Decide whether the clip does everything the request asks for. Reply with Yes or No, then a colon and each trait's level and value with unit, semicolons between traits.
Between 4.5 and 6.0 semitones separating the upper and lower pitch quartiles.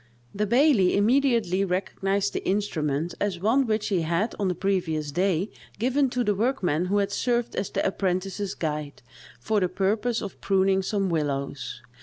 No: average, 3.4 semitones